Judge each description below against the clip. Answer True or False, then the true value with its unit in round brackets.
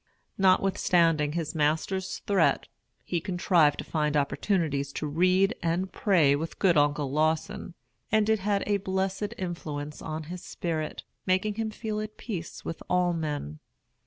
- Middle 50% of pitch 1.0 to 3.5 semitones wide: False (4.0 semitones)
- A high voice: False (175 Hz)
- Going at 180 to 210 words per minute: False (145 wpm)